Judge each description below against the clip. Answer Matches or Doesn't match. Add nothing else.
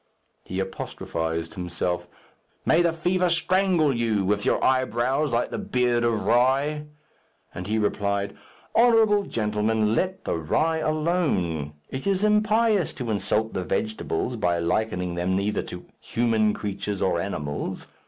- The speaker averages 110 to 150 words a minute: Matches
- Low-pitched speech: Matches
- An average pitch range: Doesn't match